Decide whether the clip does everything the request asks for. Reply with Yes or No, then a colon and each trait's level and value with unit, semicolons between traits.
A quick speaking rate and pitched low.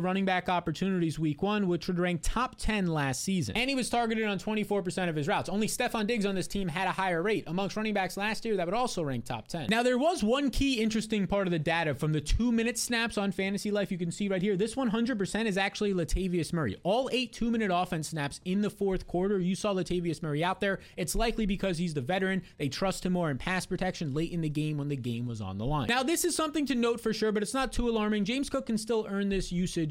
No: fast, 265 wpm; high, 195 Hz